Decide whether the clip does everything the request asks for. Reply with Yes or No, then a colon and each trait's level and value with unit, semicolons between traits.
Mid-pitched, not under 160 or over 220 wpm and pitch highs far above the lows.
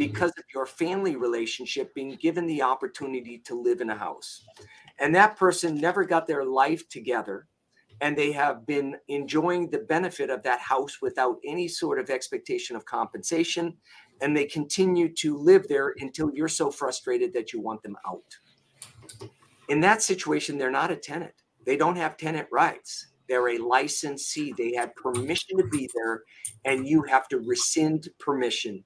Yes: medium, 160 Hz; average, 170 wpm; wide, 7.6 semitones